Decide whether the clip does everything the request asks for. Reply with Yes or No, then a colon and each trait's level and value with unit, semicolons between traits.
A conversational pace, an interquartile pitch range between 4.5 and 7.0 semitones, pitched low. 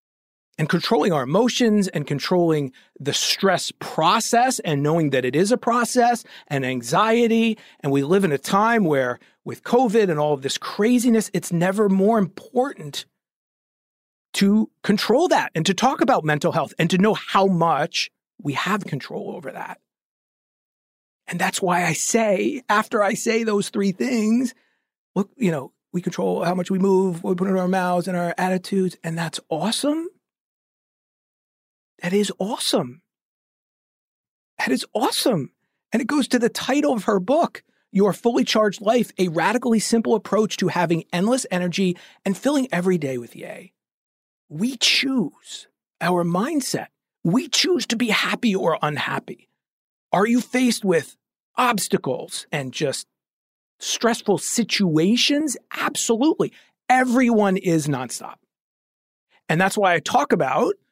No: average, 150 wpm; average, 5.2 semitones; high, 200 Hz